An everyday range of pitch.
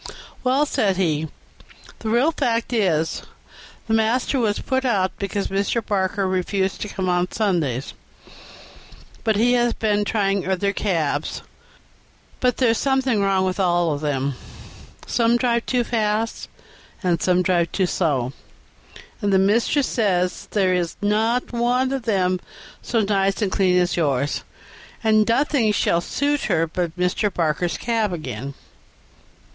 Yes: average, 4.4 semitones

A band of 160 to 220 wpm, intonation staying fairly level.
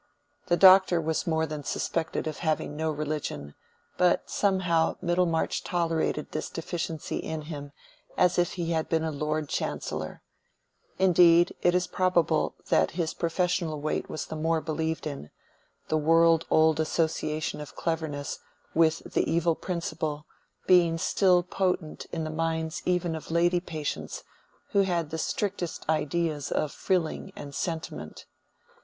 No: average, 140 wpm; narrow, 1.9 semitones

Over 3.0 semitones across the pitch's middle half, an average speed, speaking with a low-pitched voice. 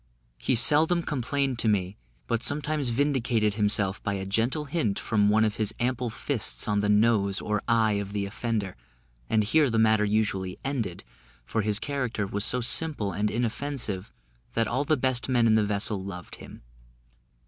Yes: average, 3.9 semitones; average, 175 wpm; low, 110 Hz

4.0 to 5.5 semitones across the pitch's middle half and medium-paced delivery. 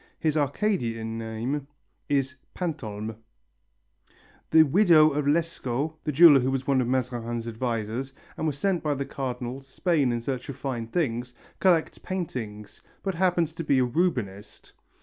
Yes: average, 5.0 semitones; average, 150 wpm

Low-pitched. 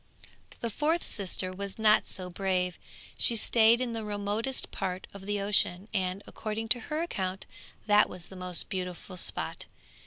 No: high, 200 Hz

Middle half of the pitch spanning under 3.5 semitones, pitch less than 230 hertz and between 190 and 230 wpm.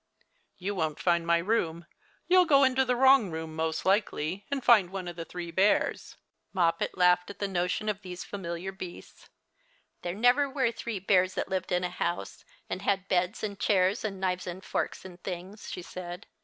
Yes: average, 3.1 semitones; medium, 185 Hz; average, 195 wpm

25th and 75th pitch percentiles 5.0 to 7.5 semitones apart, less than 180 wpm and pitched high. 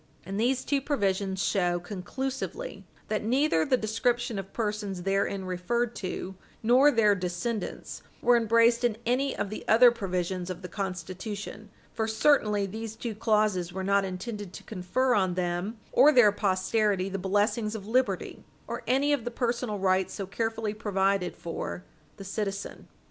No: average, 3.7 semitones; average, 155 wpm; high, 210 Hz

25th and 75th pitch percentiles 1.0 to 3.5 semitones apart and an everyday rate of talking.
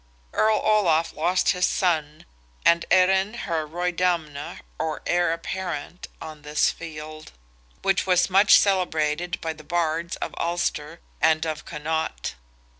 No: average, 2.7 semitones; slow, 125 wpm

